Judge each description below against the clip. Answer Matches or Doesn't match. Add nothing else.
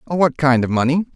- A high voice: Doesn't match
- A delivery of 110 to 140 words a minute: Doesn't match